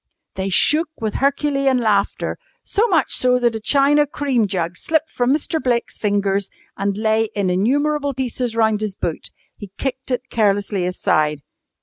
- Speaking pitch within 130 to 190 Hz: No, high, 235 Hz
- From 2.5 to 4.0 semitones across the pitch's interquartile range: No, wide, 5.5 semitones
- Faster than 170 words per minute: No, average, 155 wpm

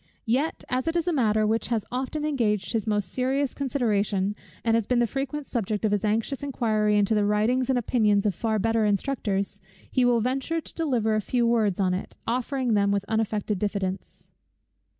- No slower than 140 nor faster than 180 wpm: No, average, 190 wpm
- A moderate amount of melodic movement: Yes, average, 3.6 semitones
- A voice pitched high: Yes, high, 225 Hz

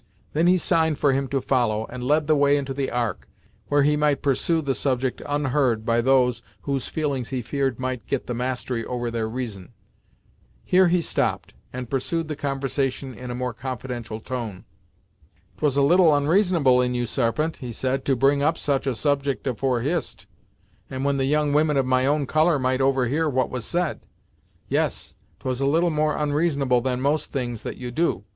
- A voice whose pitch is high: No, low, 135 Hz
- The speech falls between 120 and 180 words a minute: No, average, 190 wpm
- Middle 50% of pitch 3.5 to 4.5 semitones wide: No, average, 2.9 semitones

